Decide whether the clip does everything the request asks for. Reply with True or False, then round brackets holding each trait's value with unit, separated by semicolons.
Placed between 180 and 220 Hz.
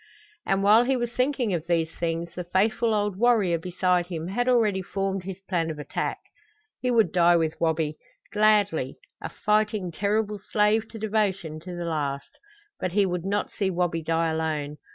True (190 Hz)